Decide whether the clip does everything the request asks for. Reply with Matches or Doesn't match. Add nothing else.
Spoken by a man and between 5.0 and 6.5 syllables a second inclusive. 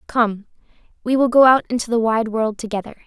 Doesn't match